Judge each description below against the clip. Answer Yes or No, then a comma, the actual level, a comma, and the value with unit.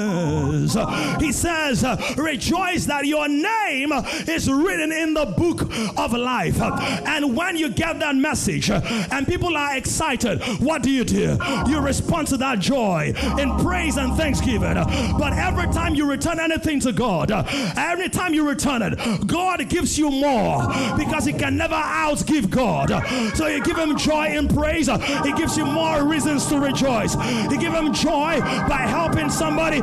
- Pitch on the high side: Yes, very high, 290 Hz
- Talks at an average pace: Yes, average, 160 wpm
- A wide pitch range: No, average, 3.8 semitones